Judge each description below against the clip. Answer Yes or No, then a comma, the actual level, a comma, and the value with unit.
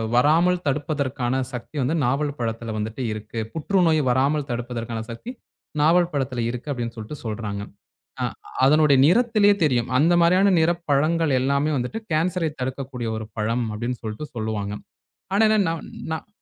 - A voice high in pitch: No, low, 135 Hz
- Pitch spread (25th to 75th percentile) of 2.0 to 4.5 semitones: No, wide, 5.4 semitones